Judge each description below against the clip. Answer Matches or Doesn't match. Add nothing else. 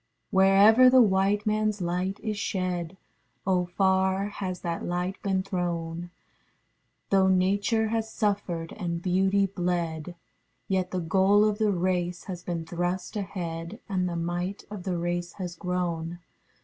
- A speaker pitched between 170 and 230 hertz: Matches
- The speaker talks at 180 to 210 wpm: Doesn't match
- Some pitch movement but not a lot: Doesn't match